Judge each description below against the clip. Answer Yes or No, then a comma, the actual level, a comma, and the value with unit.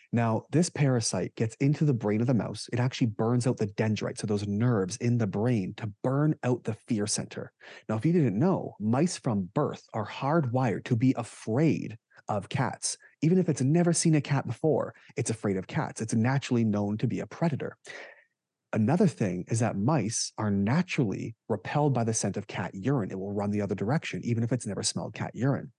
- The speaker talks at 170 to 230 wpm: Yes, fast, 205 wpm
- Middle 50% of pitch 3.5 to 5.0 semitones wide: Yes, average, 4.4 semitones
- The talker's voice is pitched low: Yes, low, 120 Hz